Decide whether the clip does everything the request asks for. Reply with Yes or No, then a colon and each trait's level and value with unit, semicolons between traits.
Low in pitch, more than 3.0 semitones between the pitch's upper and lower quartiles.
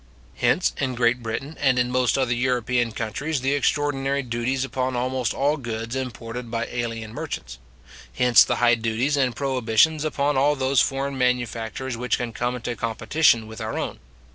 No: low, 125 Hz; narrow, 2.6 semitones